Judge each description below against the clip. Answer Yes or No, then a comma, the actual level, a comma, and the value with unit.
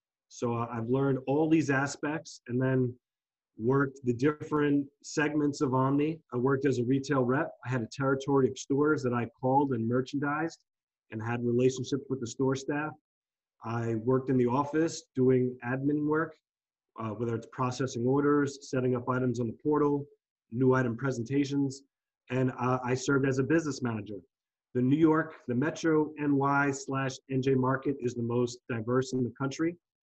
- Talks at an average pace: Yes, average, 170 wpm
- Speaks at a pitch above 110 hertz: Yes, low, 135 Hz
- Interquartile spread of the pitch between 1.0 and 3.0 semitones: Yes, narrow, 2.4 semitones